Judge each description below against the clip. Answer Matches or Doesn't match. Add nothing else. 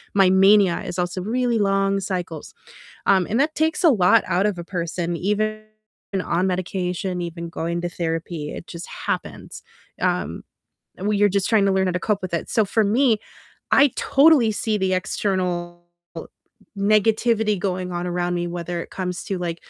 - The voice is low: Doesn't match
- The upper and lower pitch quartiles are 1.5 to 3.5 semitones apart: Matches